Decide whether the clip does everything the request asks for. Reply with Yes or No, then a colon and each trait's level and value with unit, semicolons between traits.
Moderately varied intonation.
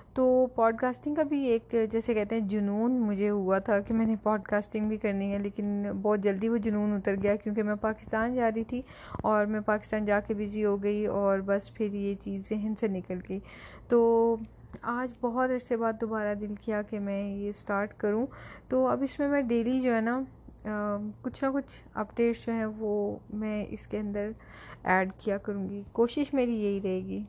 No: narrow, 2.2 semitones